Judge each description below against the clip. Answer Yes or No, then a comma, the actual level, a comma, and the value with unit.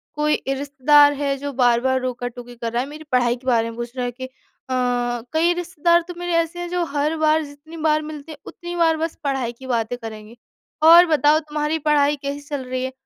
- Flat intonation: No, average, 4.1 semitones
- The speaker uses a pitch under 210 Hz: No, very high, 285 Hz